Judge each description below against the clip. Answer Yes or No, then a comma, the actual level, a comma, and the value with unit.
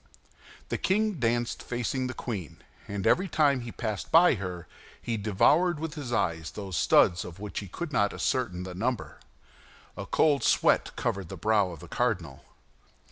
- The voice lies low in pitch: Yes, low, 110 Hz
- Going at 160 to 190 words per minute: Yes, average, 170 wpm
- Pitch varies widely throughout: Yes, wide, 6.7 semitones